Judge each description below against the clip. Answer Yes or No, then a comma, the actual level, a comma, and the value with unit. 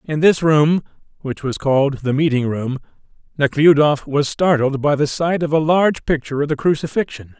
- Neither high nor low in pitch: Yes, medium, 145 Hz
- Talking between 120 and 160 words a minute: No, average, 180 wpm